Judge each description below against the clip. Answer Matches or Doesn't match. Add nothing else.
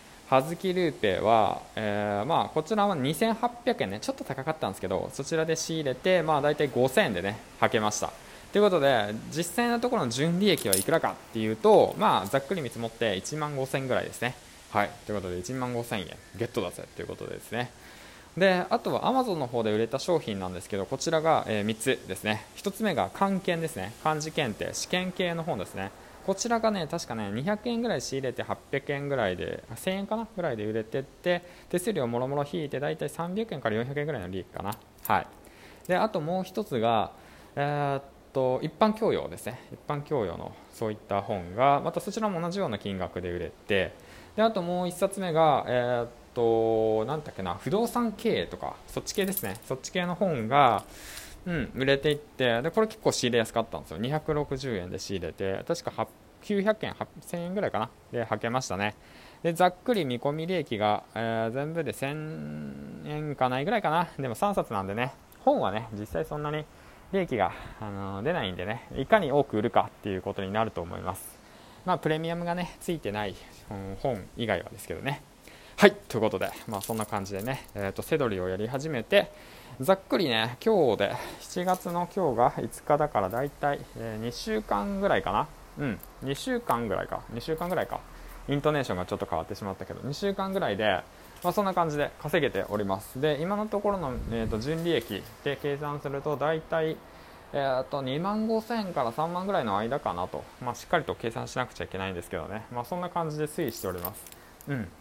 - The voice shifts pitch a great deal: Matches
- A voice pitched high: Doesn't match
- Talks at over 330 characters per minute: Matches